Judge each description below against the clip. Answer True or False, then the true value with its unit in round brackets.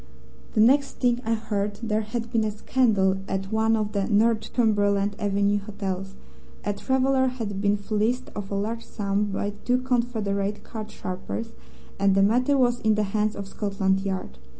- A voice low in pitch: False (210 Hz)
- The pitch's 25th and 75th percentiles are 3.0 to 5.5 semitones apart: False (2.5 semitones)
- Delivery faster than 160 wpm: True (170 wpm)